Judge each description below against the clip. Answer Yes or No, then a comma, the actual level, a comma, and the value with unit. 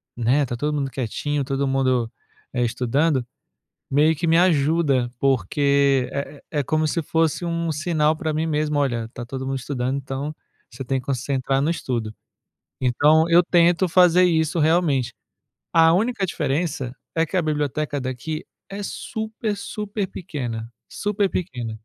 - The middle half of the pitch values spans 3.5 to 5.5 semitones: Yes, average, 3.9 semitones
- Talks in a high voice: No, medium, 150 Hz